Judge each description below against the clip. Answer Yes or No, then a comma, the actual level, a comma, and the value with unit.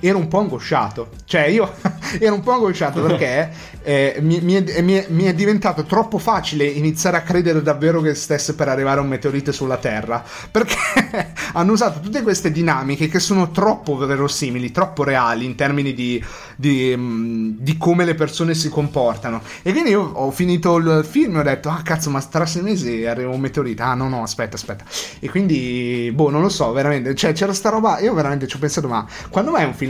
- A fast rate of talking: Yes, fast, 205 wpm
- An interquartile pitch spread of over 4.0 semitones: Yes, average, 5.2 semitones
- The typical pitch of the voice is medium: Yes, medium, 150 Hz